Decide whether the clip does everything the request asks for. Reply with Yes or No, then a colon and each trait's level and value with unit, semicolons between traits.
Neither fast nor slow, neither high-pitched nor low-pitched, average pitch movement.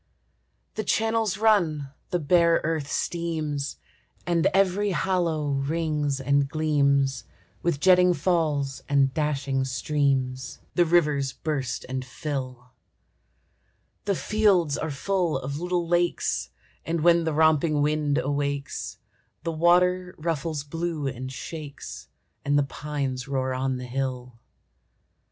No: slow, 120 wpm; medium, 150 Hz; average, 3.7 semitones